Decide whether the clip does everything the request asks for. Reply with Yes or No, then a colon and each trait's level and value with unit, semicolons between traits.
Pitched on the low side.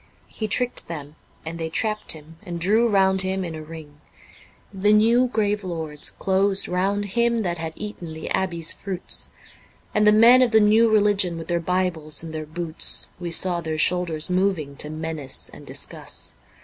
No: medium, 180 Hz